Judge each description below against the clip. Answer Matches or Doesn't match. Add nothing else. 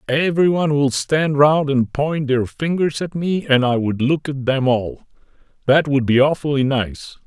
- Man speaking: Matches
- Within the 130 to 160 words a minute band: Doesn't match